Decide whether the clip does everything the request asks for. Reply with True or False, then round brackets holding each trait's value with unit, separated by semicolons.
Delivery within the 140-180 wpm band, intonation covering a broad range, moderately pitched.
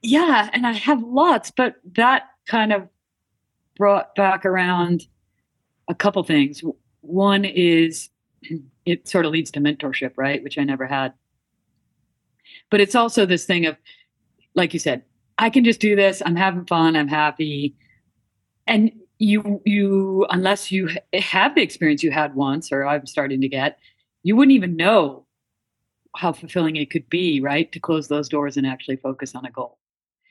True (165 wpm; 6.1 semitones; 170 Hz)